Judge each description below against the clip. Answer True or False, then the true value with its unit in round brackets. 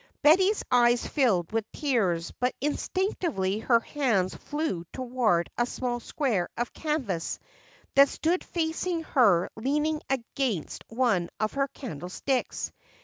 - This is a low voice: False (250 Hz)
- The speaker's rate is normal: False (120 wpm)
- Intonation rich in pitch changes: True (6.3 semitones)